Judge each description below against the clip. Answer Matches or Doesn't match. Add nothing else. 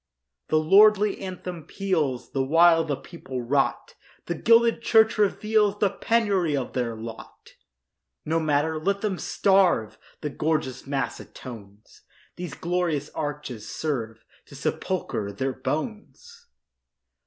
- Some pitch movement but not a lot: Doesn't match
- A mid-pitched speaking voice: Matches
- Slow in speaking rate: Matches